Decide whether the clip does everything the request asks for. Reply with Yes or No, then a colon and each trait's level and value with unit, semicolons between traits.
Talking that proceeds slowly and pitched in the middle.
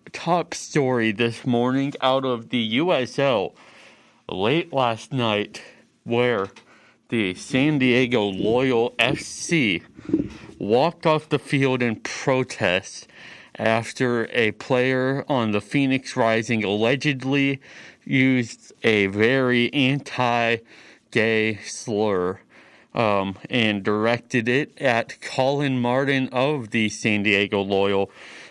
No: slow, 105 wpm; low, 120 Hz